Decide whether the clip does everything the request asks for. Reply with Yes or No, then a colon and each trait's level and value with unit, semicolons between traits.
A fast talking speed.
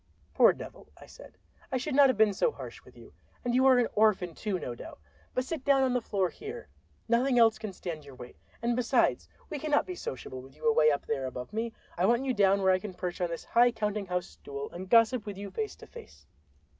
Yes: fast, 235 wpm